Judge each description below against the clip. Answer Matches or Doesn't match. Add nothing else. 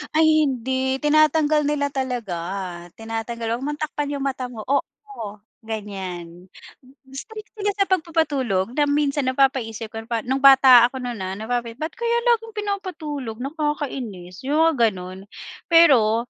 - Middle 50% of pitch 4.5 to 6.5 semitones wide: Matches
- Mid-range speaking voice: Doesn't match